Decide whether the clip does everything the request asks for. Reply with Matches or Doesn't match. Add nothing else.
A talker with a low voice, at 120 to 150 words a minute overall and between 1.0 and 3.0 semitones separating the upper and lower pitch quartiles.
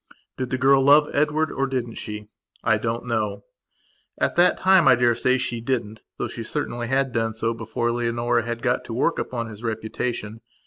Doesn't match